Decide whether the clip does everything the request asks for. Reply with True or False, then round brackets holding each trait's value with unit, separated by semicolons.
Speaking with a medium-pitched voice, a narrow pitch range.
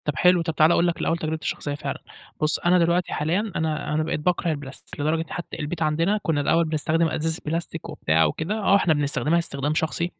True (160 Hz; 2.1 semitones)